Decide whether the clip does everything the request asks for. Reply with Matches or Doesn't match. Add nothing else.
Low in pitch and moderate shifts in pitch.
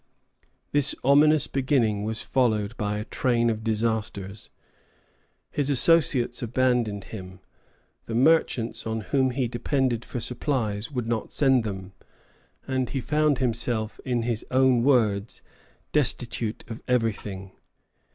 Matches